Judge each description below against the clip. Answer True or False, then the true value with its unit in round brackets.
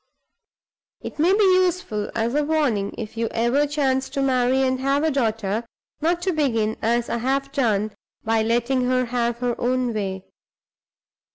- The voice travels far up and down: False (3.7 semitones)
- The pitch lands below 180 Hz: False (250 Hz)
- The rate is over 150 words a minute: True (165 wpm)